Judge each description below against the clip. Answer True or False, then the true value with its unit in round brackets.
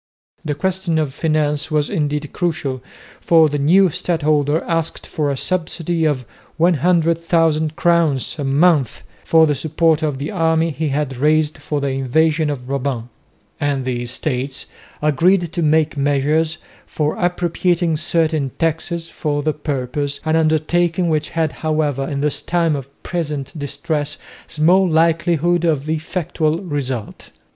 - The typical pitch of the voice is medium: True (155 Hz)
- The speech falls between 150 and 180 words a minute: False (140 wpm)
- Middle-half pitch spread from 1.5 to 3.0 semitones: True (2.5 semitones)